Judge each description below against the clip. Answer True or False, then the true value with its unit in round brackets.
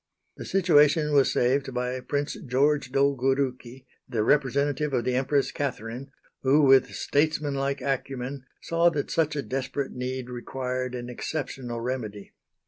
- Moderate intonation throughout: False (2.3 semitones)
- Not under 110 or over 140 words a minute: True (135 wpm)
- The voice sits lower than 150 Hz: True (135 Hz)